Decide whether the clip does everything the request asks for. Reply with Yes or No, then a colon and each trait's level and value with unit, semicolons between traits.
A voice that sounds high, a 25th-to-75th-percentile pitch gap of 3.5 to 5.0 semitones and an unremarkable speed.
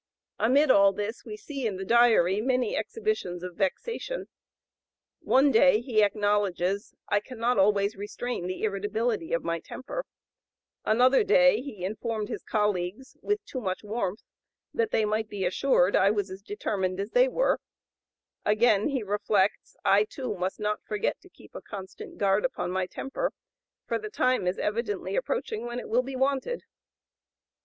Yes: high, 215 Hz; average, 4.6 semitones; average, 160 wpm